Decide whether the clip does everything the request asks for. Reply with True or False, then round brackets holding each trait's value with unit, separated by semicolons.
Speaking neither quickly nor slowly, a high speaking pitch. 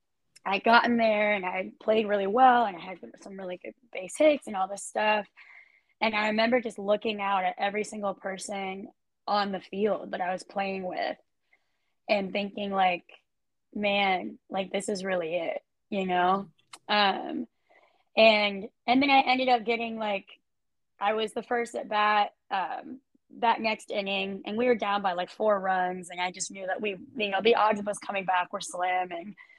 True (190 wpm; 205 Hz)